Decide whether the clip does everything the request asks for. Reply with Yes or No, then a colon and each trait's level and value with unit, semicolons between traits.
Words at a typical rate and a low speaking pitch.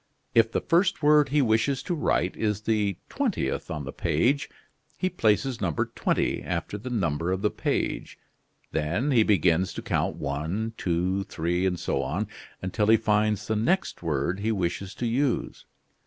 Yes: average, 170 wpm; low, 105 Hz